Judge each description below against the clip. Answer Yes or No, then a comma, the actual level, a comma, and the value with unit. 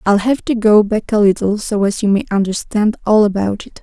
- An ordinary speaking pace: No, fast, 235 wpm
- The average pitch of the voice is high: Yes, high, 210 Hz